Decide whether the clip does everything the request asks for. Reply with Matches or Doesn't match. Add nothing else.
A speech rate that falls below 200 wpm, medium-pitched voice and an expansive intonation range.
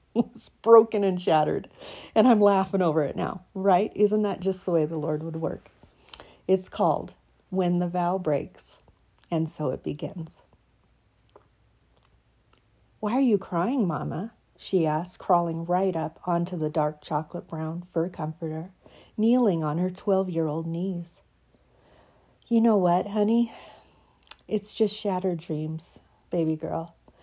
Doesn't match